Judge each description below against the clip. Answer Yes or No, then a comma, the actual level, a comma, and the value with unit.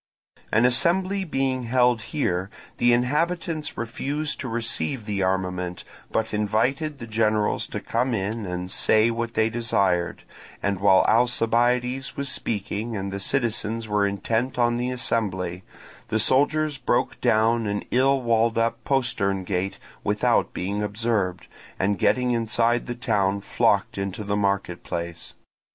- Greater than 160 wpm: No, average, 140 wpm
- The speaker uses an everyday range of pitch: Yes, average, 3.7 semitones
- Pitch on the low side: Yes, low, 115 Hz